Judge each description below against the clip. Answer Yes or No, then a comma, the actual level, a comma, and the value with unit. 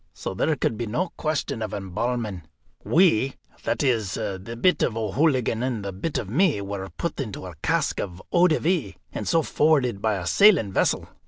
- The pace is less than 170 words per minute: No, average, 190 wpm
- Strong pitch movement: Yes, wide, 7.6 semitones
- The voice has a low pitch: Yes, low, 120 Hz